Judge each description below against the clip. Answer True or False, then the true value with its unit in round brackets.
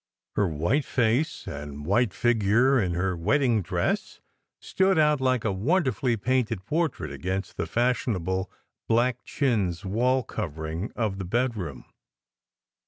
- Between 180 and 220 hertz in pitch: False (110 Hz)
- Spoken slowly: True (130 wpm)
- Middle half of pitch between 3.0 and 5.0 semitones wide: False (5.4 semitones)